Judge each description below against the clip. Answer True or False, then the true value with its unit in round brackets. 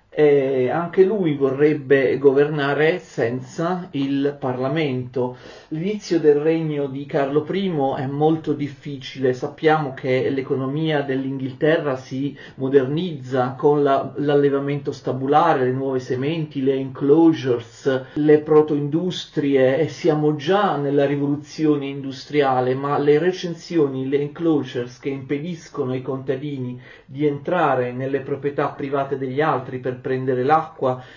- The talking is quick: False (115 wpm)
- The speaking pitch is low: False (145 Hz)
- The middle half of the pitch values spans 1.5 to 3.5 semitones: True (2.4 semitones)